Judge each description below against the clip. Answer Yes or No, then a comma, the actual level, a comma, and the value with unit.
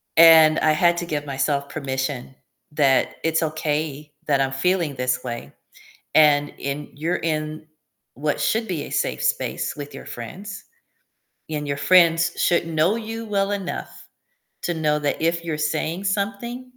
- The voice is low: No, medium, 155 Hz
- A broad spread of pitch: No, average, 3.4 semitones